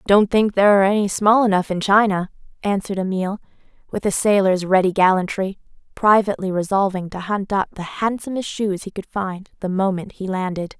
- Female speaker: Yes, female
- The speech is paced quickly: No, average, 170 wpm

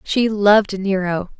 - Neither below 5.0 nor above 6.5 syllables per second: No, 4.0 syllables/s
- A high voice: Yes, high, 200 Hz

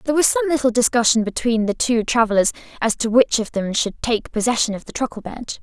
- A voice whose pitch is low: No, high, 235 Hz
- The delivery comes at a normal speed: No, fast, 225 wpm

